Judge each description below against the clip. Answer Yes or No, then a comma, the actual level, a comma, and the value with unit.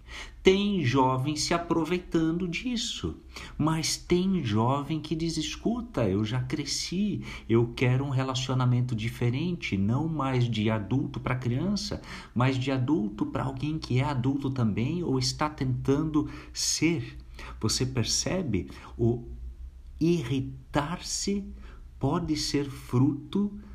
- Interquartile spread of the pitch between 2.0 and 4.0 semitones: No, average, 5.1 semitones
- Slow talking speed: Yes, slow, 115 wpm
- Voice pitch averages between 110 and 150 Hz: Yes, low, 135 Hz